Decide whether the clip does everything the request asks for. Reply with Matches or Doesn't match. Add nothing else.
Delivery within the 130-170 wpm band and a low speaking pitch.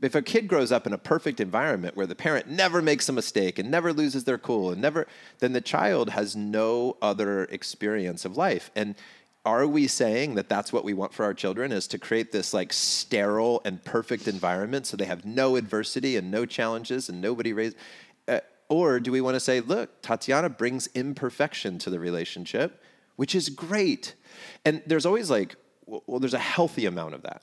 Doesn't match